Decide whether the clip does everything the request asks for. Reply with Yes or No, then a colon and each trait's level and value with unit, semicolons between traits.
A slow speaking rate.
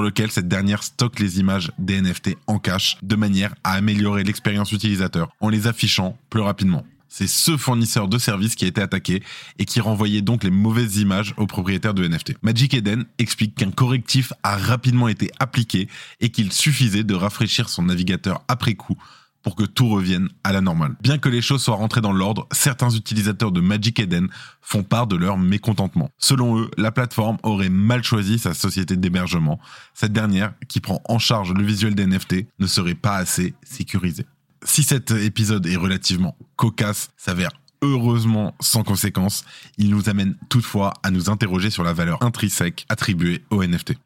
No: average, 180 wpm